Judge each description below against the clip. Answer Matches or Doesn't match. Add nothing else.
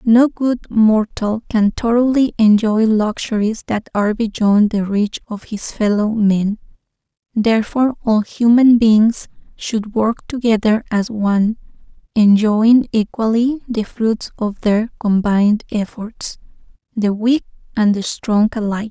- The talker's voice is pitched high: Matches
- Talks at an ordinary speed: Doesn't match